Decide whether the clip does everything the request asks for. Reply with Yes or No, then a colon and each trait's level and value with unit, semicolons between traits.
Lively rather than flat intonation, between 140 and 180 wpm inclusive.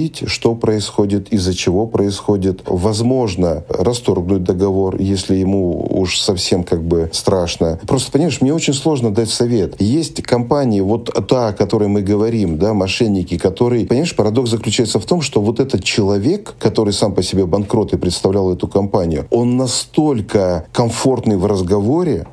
No: average, 3.8 semitones; average, 150 wpm